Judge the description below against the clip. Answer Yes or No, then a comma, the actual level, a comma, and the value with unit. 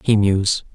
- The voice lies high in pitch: No, low, 100 Hz